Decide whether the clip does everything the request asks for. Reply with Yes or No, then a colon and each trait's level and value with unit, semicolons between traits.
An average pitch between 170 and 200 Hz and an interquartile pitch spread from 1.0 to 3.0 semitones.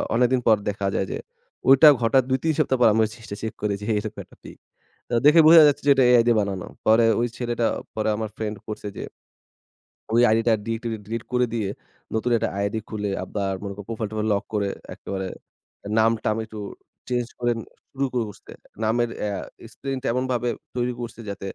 No: low, 115 Hz; average, 2.7 semitones